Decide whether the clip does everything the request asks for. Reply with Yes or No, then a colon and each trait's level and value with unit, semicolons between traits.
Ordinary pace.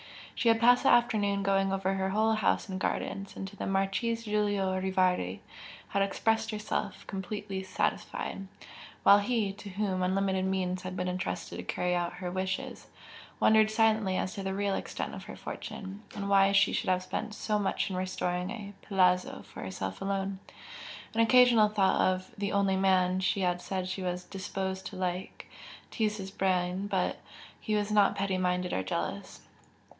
Yes: average, 175 wpm